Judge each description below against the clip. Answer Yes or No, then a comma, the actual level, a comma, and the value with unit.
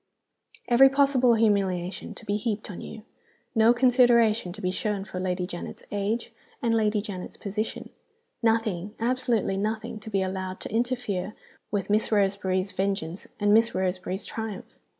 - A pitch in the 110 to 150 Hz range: No, high, 210 Hz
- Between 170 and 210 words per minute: No, average, 150 wpm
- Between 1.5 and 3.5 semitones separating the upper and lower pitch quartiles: Yes, average, 3.1 semitones